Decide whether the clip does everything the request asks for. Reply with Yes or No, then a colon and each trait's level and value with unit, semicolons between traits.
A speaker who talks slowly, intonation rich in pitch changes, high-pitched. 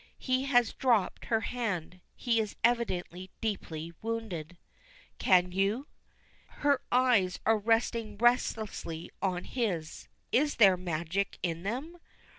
No: slow, 115 wpm; average, 4.9 semitones; high, 215 Hz